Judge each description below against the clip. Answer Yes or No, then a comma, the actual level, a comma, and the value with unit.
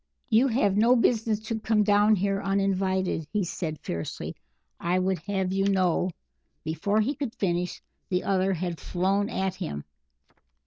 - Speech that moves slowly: No, average, 160 wpm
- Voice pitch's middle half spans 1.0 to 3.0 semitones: Yes, narrow, 2.6 semitones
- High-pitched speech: Yes, high, 195 Hz